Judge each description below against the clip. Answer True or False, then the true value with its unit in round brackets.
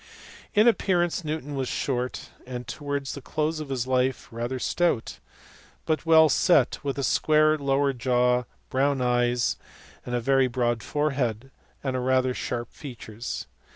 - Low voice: True (130 Hz)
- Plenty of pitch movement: False (3.3 semitones)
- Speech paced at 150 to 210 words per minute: False (140 wpm)